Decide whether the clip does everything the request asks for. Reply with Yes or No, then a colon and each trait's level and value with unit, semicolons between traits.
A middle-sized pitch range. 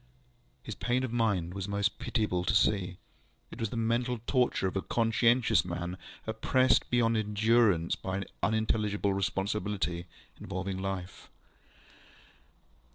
Yes: average, 3.3 semitones